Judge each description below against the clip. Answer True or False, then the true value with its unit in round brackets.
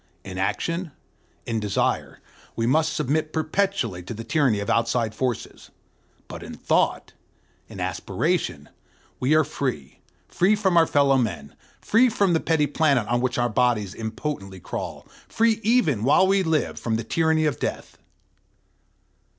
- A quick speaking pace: False (145 wpm)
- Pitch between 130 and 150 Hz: True (140 Hz)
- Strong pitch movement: True (6.3 semitones)